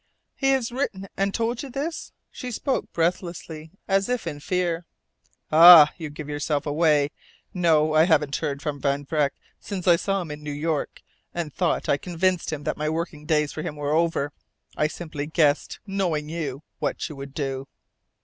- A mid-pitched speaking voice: Yes, medium, 160 Hz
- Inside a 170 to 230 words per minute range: Yes, average, 180 wpm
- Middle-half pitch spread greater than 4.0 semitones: No, average, 3.5 semitones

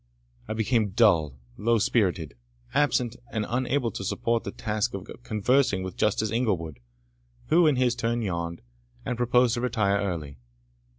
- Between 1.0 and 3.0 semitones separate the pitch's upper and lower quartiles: No, average, 4.3 semitones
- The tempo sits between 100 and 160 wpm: Yes, average, 150 wpm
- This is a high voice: No, low, 110 Hz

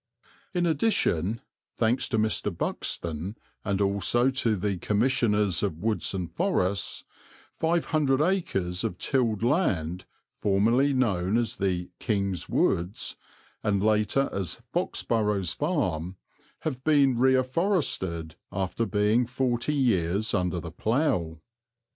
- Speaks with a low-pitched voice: Yes, low, 105 Hz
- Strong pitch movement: Yes, wide, 5.9 semitones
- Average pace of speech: No, slow, 120 wpm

